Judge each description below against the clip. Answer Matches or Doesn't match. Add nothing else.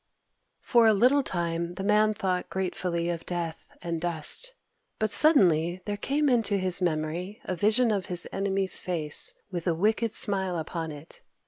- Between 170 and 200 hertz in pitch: Matches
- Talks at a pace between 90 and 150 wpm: Doesn't match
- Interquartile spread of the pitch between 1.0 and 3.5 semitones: Doesn't match